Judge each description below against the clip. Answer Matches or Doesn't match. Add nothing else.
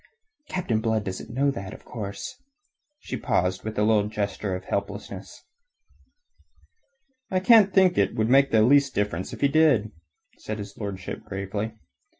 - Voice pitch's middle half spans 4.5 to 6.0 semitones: Matches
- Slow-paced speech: Doesn't match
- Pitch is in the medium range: Doesn't match